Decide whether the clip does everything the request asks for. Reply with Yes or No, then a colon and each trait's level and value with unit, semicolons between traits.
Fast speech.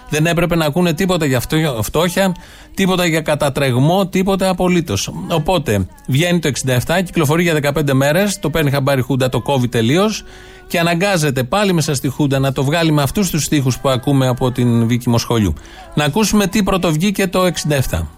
Yes: fast, 180 wpm